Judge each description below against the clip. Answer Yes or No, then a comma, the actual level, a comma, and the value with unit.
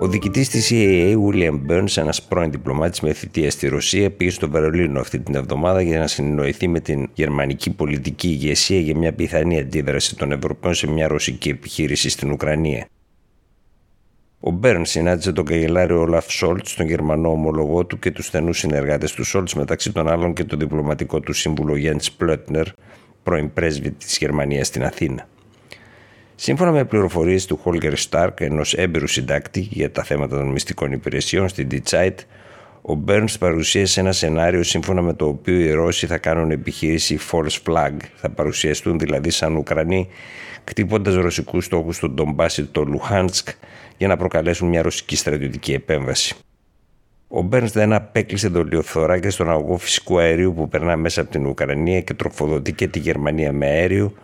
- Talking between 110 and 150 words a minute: No, average, 165 wpm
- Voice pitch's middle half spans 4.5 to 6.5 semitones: No, average, 3.6 semitones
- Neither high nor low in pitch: No, very low, 85 Hz